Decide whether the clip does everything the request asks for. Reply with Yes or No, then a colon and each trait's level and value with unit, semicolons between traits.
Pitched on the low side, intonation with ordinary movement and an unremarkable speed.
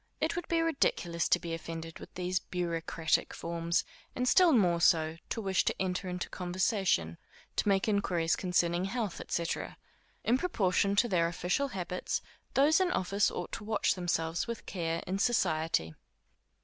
No: medium, 180 Hz; average, 3.7 semitones; average, 160 wpm